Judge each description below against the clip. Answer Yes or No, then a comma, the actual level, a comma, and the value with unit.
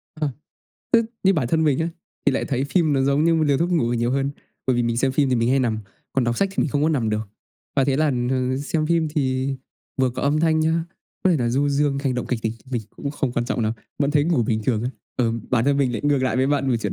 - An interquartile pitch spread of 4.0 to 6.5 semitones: No, average, 3.5 semitones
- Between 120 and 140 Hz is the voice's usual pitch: Yes, low, 135 Hz